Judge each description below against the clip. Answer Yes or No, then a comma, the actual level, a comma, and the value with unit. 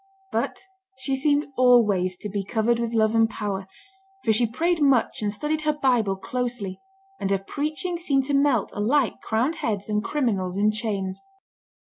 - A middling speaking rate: Yes, average, 165 wpm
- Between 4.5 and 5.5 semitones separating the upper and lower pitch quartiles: Yes, average, 5.2 semitones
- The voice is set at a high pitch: Yes, high, 230 Hz